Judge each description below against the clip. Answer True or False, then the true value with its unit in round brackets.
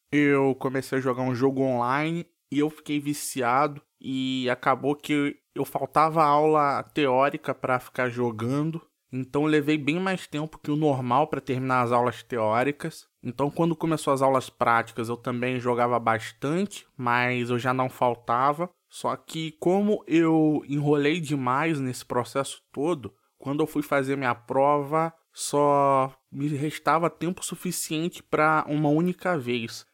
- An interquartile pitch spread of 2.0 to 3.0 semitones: False (3.4 semitones)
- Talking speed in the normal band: True (150 wpm)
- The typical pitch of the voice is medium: True (145 Hz)